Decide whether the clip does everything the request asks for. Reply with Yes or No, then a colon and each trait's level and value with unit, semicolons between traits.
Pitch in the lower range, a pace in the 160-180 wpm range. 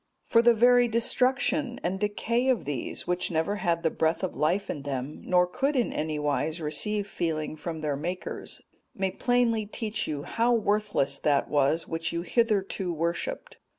No: medium, 185 Hz; average, 170 wpm